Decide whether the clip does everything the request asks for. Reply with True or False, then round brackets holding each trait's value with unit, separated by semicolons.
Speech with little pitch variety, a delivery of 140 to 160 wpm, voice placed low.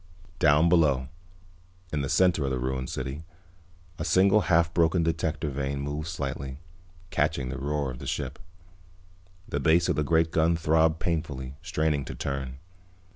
False (3.3 semitones; 155 wpm; 75 Hz)